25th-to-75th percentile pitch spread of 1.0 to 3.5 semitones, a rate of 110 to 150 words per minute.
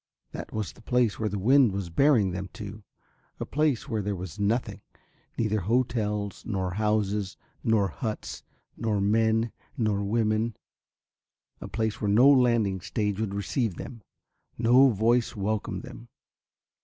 Yes: narrow, 2.5 semitones; average, 145 wpm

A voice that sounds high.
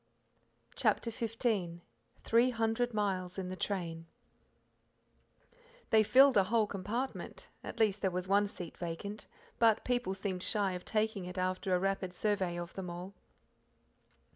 Yes: high, 195 Hz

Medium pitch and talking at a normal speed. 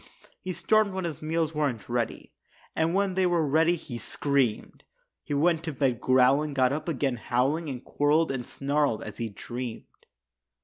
Yes: medium, 145 Hz; average, 170 wpm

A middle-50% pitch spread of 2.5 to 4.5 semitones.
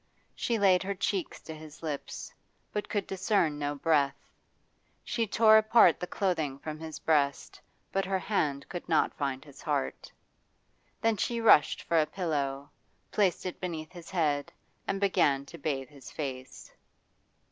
No: average, 5.2 semitones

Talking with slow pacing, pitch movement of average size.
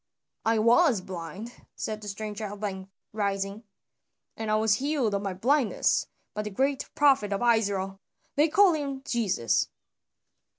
No: average, 145 wpm; average, 4.6 semitones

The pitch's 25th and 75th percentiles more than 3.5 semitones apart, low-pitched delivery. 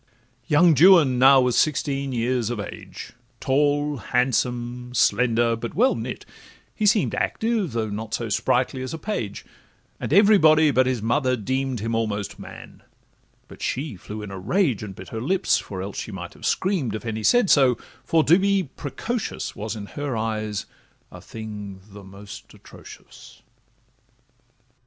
Yes: wide, 5.4 semitones; low, 125 Hz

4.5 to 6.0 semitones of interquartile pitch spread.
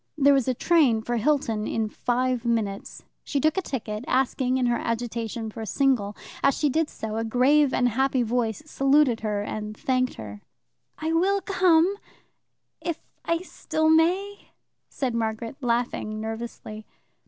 Yes: average, 4.9 semitones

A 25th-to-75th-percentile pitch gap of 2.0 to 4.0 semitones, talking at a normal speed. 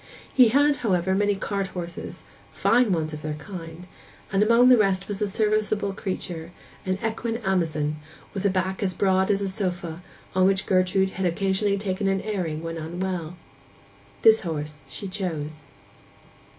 Yes: average, 3.1 semitones; average, 160 wpm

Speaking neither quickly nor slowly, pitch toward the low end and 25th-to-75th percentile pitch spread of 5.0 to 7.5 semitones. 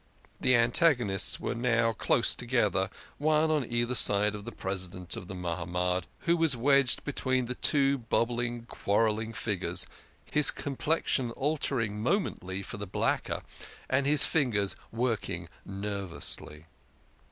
No: slow, 130 wpm; low, 115 Hz; wide, 5.6 semitones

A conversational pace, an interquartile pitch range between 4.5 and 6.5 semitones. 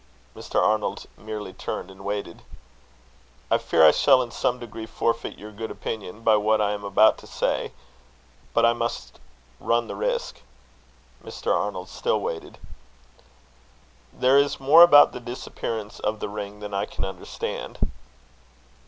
No: average, 150 wpm; average, 3.3 semitones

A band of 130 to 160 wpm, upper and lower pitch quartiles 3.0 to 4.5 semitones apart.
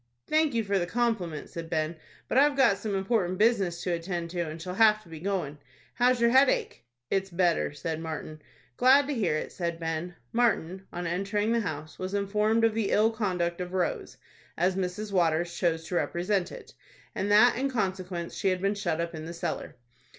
No: average, 200 wpm; average, 4.1 semitones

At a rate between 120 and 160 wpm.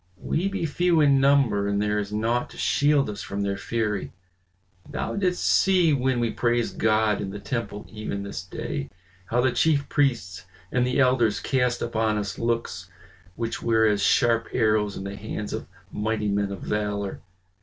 No: average, 175 wpm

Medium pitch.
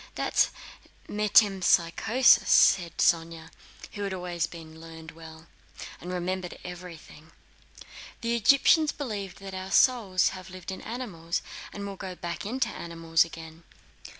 Yes: medium, 180 Hz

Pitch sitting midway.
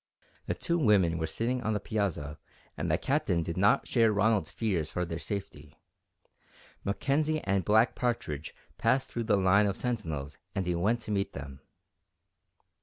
No: low, 100 Hz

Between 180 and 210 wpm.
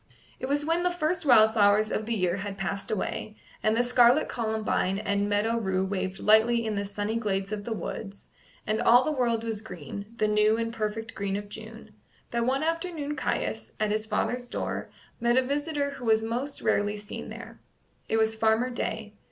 Yes: average, 195 wpm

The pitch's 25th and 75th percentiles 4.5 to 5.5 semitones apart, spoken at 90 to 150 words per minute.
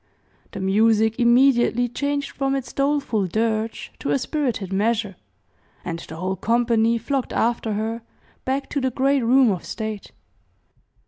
No: average, 3.7 semitones; average, 140 wpm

